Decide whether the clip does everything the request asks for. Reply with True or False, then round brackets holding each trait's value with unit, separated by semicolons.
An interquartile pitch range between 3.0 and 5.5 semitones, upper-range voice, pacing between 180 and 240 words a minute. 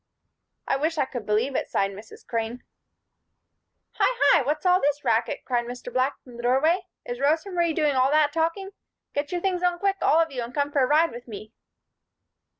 True (5.1 semitones; 285 Hz; 205 wpm)